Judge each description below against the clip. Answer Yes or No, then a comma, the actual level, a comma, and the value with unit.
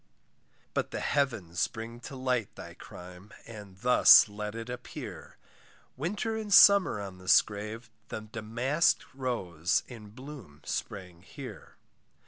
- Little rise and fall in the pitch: No, average, 4.5 semitones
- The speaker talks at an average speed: No, slow, 125 wpm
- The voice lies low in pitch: Yes, low, 115 Hz